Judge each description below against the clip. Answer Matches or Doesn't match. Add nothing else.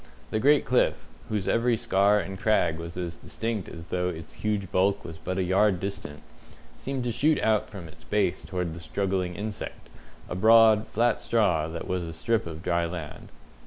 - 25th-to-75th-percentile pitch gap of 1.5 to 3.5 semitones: Doesn't match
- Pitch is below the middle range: Matches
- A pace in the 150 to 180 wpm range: Doesn't match